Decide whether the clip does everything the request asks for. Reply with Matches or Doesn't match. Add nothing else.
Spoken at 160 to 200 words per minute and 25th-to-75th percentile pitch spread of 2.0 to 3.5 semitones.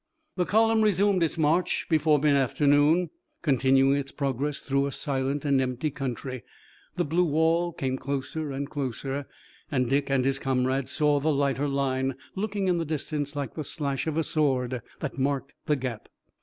Matches